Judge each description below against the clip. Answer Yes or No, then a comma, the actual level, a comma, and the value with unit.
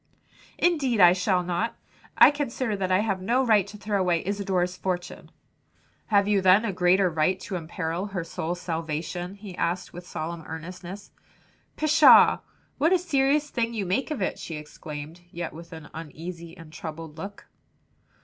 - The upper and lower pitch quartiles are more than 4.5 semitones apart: No, average, 3.7 semitones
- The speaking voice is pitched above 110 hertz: Yes, medium, 185 Hz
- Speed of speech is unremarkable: Yes, average, 165 wpm